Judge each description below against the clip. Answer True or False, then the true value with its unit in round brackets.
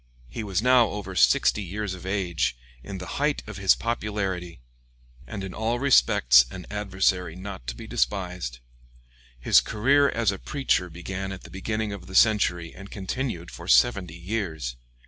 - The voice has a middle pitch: False (95 Hz)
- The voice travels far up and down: False (3.3 semitones)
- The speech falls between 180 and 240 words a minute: False (165 wpm)